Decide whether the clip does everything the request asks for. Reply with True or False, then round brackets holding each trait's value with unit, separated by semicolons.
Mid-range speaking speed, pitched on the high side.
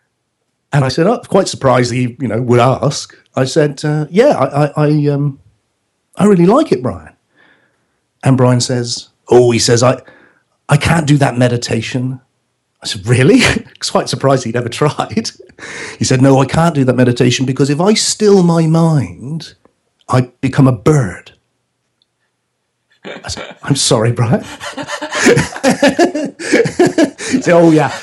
False (150 wpm; 135 Hz)